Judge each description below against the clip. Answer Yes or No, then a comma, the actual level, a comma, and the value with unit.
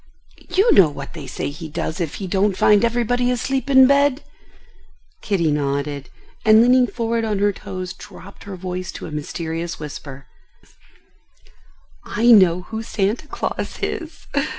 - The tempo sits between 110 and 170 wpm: Yes, average, 150 wpm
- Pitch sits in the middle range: No, high, 195 Hz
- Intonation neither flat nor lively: No, wide, 6.5 semitones